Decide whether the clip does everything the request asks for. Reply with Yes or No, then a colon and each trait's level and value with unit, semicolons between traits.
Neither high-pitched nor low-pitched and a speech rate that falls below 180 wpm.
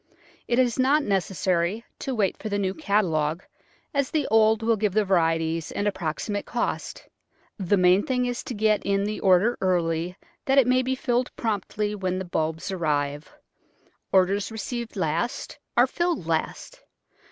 No: high, 205 Hz; average, 160 wpm